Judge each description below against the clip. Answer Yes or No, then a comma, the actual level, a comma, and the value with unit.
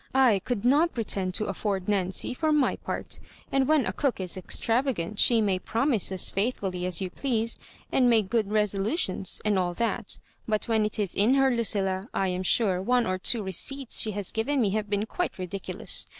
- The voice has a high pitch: Yes, high, 210 Hz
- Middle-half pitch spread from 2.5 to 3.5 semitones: No, average, 4.2 semitones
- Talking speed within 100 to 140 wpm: No, fast, 205 wpm